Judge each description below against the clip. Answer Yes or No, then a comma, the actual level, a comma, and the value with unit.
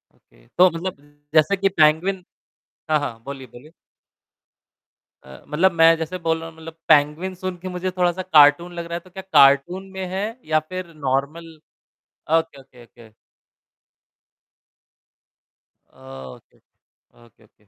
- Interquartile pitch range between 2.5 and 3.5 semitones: No, average, 4.6 semitones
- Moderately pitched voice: Yes, medium, 165 Hz